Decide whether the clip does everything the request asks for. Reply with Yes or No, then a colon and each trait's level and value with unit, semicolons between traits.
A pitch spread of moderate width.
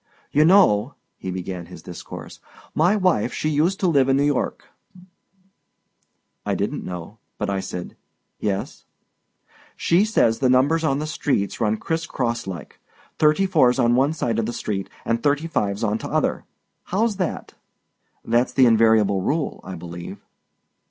No: wide, 6.9 semitones